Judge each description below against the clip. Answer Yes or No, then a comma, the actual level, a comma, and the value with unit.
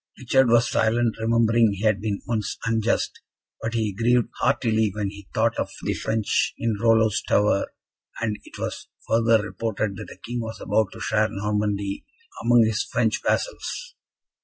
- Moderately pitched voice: No, low, 110 Hz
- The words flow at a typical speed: Yes, average, 160 wpm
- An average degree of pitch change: No, narrow, 1.8 semitones